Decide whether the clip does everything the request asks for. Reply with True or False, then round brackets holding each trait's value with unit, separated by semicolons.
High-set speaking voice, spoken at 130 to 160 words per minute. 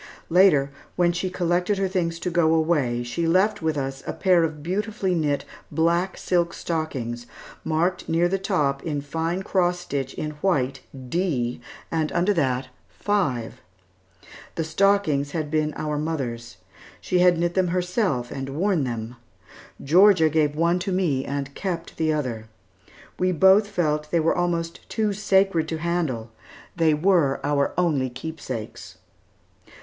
False (165 Hz; 150 wpm)